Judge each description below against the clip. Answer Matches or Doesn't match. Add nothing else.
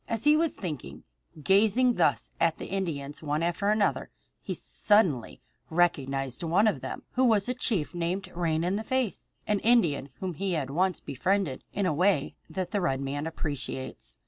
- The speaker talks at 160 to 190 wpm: Matches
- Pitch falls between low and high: Matches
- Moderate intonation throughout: Doesn't match